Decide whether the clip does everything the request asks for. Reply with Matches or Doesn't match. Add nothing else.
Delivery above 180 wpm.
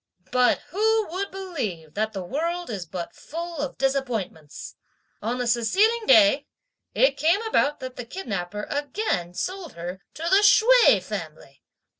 Doesn't match